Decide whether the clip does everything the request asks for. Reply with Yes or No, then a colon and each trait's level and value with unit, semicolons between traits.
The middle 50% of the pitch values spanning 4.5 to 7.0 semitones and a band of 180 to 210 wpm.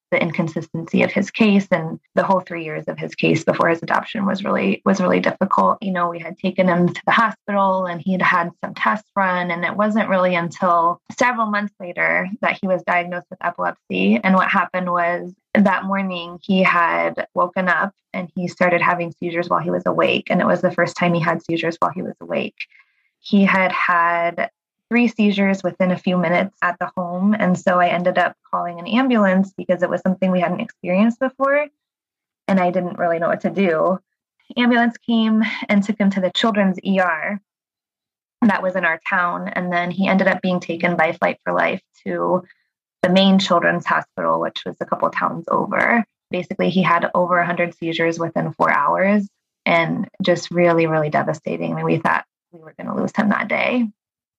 No: narrow, 2.5 semitones; average, 200 wpm